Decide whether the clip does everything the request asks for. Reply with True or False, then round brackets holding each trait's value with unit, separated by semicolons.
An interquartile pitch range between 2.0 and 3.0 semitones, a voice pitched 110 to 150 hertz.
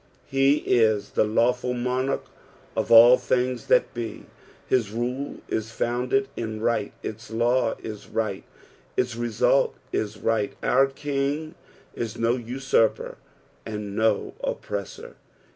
True (2.4 semitones; 120 Hz)